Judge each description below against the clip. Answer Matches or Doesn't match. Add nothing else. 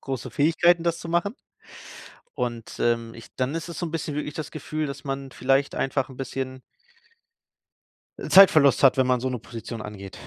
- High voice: Doesn't match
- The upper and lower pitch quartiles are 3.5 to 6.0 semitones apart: Matches